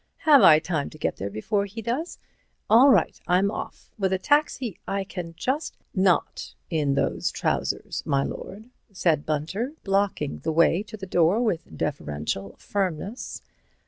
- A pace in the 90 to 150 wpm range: No, average, 160 wpm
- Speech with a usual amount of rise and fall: No, wide, 5.8 semitones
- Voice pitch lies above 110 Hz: Yes, high, 190 Hz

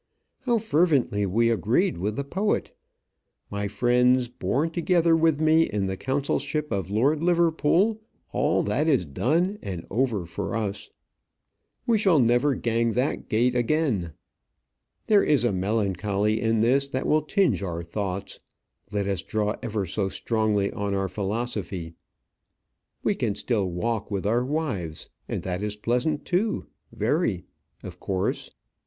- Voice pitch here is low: Yes, low, 115 Hz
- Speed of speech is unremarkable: Yes, average, 145 wpm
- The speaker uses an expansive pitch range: Yes, wide, 7.0 semitones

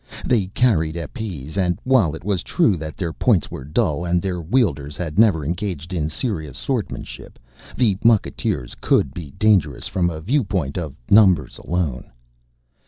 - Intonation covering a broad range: No, average, 4.9 semitones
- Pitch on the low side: Yes, very low, 85 Hz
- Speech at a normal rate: Yes, average, 155 wpm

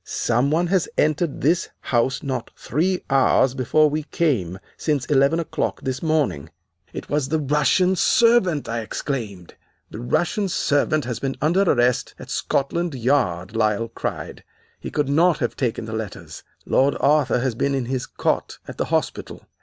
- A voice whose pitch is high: No, medium, 140 Hz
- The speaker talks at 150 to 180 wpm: Yes, average, 160 wpm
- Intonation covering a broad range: No, average, 4.3 semitones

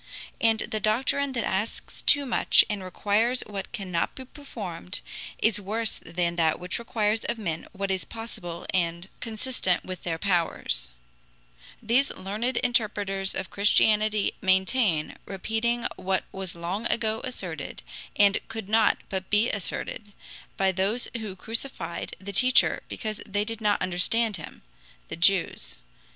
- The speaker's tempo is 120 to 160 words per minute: Yes, average, 140 wpm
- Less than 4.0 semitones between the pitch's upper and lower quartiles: Yes, average, 3.4 semitones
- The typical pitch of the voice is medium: No, high, 205 Hz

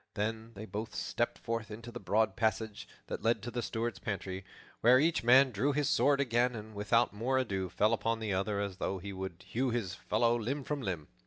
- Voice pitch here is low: Yes, low, 110 Hz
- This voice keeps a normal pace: No, fast, 215 wpm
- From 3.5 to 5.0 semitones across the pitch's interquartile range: No, average, 2.9 semitones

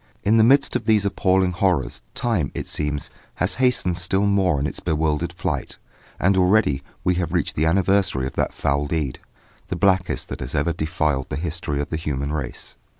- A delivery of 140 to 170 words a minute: No, average, 190 wpm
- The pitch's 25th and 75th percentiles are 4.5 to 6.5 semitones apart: Yes, average, 4.8 semitones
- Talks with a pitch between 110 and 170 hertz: No, very low, 85 Hz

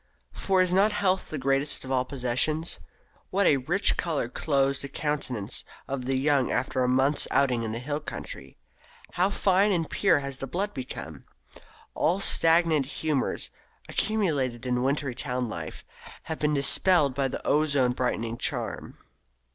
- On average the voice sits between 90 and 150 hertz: Yes, medium, 140 Hz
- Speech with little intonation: No, average, 4.3 semitones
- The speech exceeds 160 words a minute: No, average, 155 wpm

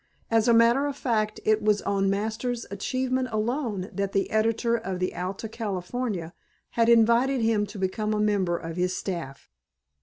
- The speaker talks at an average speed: Yes, average, 170 wpm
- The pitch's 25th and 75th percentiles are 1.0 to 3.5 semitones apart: Yes, average, 3.2 semitones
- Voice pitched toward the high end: Yes, high, 215 Hz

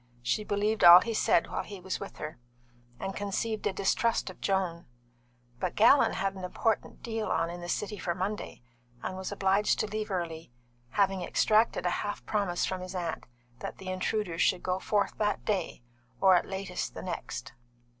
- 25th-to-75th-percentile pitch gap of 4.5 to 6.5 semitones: No, average, 2.7 semitones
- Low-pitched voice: No, high, 190 Hz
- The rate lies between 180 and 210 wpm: Yes, average, 185 wpm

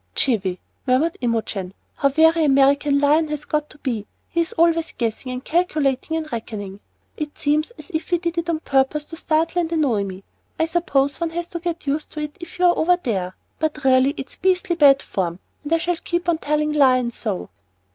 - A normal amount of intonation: Yes, average, 4.2 semitones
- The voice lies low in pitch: No, very high, 300 Hz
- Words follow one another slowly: No, average, 200 wpm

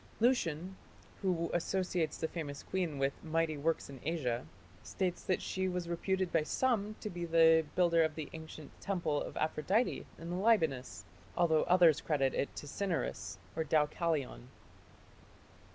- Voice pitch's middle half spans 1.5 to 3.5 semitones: Yes, average, 3.2 semitones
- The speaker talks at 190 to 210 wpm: No, average, 150 wpm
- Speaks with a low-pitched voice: No, medium, 165 Hz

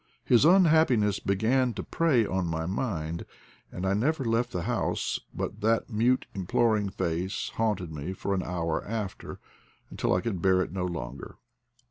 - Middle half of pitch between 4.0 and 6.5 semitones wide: Yes, average, 4.7 semitones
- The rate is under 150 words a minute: No, average, 160 wpm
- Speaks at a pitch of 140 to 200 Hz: No, low, 100 Hz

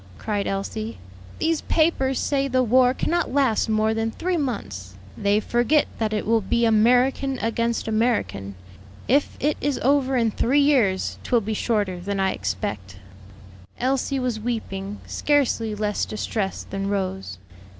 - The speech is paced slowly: No, average, 145 wpm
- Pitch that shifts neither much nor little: Yes, average, 4.5 semitones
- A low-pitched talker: No, high, 225 Hz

